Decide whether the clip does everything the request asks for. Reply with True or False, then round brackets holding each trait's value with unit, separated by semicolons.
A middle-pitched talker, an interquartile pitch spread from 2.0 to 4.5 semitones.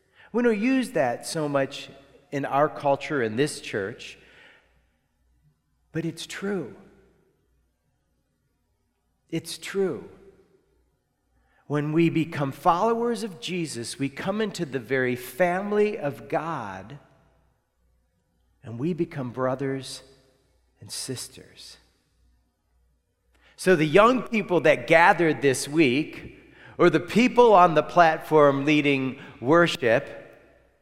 False (150 Hz; 5.4 semitones)